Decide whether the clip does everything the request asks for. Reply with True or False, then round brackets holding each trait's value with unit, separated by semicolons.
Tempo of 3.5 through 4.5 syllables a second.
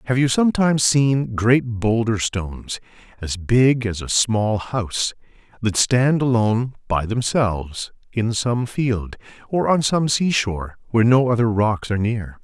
True (4.3 syllables/s)